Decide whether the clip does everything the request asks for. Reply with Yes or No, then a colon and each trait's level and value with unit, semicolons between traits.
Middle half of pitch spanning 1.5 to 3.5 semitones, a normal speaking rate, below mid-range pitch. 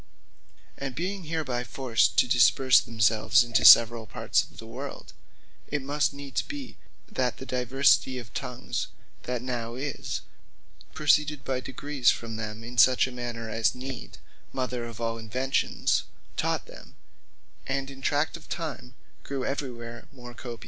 Yes: average, 2.7 semitones; average, 150 wpm; low, 125 Hz